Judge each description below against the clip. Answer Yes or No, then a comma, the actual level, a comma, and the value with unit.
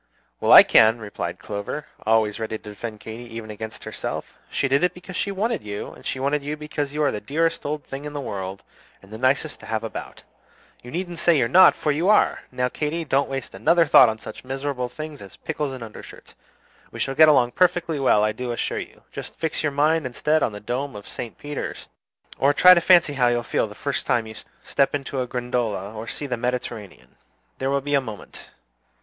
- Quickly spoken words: Yes, fast, 220 wpm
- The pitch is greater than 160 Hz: No, low, 135 Hz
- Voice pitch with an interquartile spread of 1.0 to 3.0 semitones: No, average, 5.1 semitones